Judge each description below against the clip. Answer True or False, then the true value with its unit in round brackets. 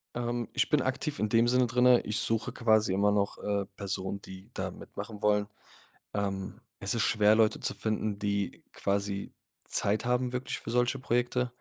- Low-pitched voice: True (110 Hz)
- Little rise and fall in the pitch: False (3.3 semitones)